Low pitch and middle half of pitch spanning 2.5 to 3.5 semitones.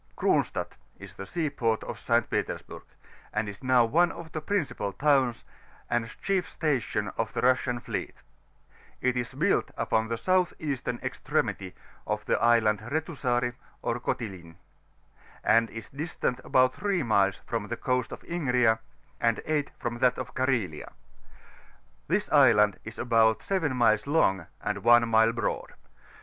No: low, 120 Hz; average, 4.3 semitones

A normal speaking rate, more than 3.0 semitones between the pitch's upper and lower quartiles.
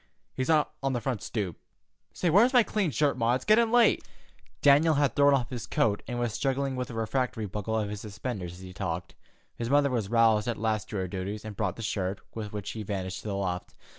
No: fast, 230 wpm; average, 5.1 semitones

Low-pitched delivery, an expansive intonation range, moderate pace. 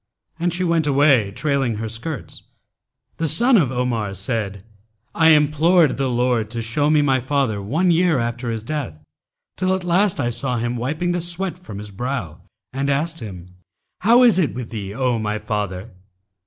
Yes: low, 130 Hz; wide, 6.3 semitones; average, 180 wpm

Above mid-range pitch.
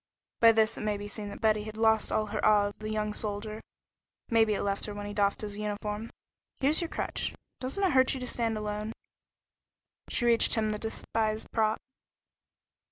Yes: high, 215 Hz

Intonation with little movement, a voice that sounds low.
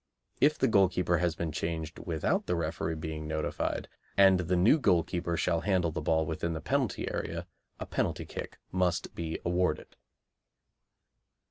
Yes: narrow, 2.2 semitones; very low, 85 Hz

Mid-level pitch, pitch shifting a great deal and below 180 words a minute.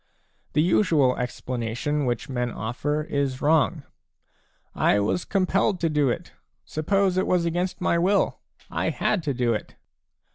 Yes: medium, 150 Hz; wide, 5.8 semitones; average, 150 wpm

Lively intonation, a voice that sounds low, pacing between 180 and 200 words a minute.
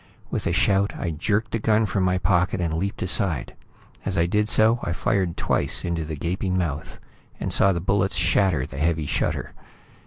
No: average, 3.0 semitones; very low, 90 Hz; average, 190 wpm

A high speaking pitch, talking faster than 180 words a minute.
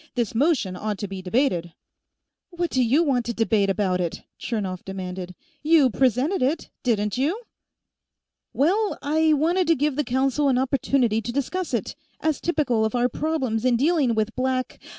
No: very high, 255 Hz; average, 170 wpm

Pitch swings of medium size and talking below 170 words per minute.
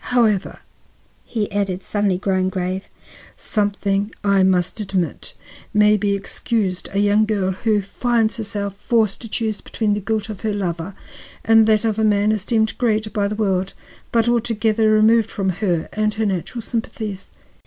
No: narrow, 2.1 semitones; average, 160 wpm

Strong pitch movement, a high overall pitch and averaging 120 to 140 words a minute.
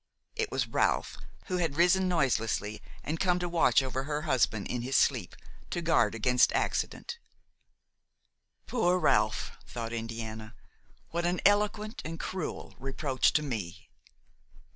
No: wide, 7.2 semitones; medium, 150 Hz; slow, 135 wpm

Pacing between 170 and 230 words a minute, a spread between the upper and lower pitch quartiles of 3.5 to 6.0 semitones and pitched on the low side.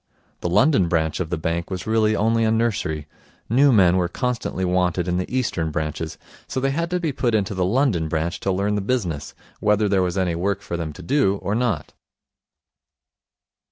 Yes: average, 195 wpm; average, 4.9 semitones; very low, 95 Hz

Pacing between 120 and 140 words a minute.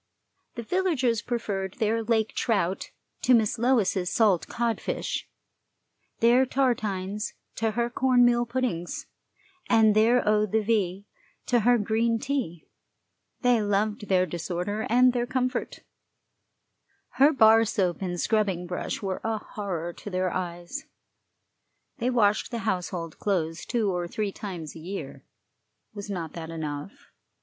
Yes: slow, 135 wpm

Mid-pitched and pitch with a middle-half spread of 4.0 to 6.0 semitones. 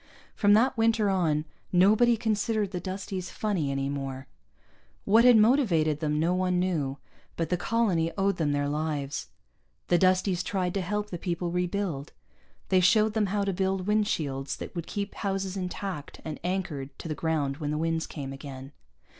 Yes: medium, 180 Hz; average, 4.8 semitones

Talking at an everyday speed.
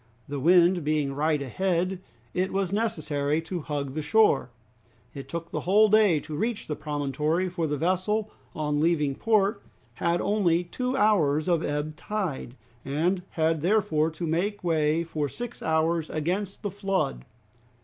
Yes: average, 155 wpm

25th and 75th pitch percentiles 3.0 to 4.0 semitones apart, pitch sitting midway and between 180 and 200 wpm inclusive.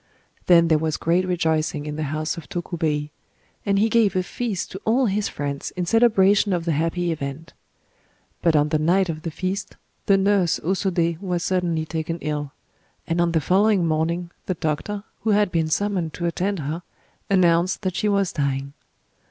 Yes: average, 3.5 semitones; medium, 170 Hz; average, 185 wpm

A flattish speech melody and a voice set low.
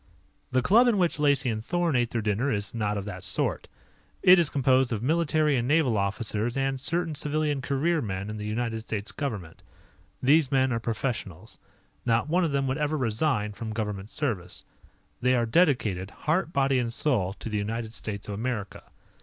No: wide, 5.4 semitones; low, 125 Hz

